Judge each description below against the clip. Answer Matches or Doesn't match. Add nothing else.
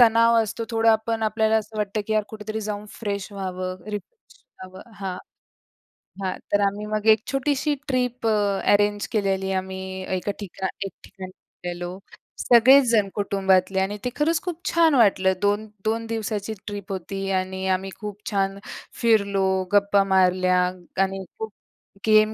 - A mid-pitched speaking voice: Doesn't match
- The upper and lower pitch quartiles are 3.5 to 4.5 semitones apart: Doesn't match